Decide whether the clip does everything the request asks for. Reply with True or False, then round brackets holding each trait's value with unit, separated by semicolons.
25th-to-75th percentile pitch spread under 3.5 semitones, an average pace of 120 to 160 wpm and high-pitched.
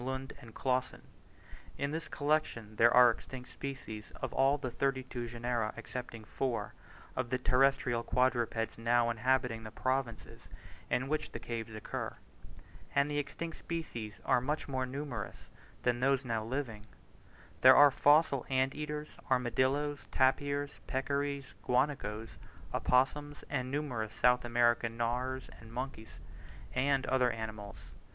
False (2.9 semitones; 135 wpm; 130 Hz)